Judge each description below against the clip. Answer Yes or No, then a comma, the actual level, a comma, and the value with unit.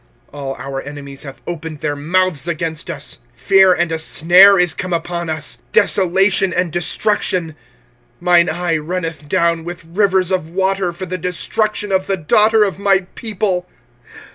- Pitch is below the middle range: No, medium, 175 Hz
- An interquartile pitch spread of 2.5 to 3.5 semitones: Yes, average, 2.9 semitones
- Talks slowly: No, average, 165 wpm